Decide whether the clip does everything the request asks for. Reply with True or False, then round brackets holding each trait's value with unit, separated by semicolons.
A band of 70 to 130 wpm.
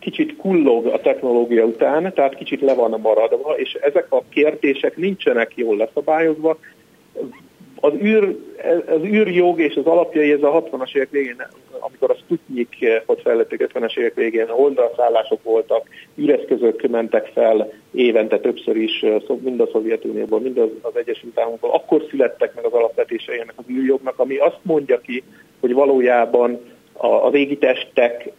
False (150 wpm)